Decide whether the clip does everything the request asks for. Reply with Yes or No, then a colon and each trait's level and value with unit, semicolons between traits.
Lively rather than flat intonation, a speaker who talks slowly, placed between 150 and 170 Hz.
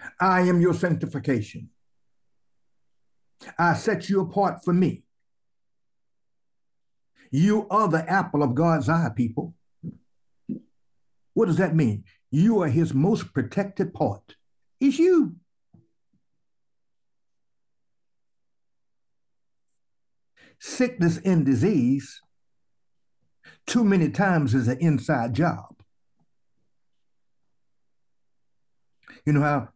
Yes: wide, 6.6 semitones; slow, 85 wpm; medium, 160 Hz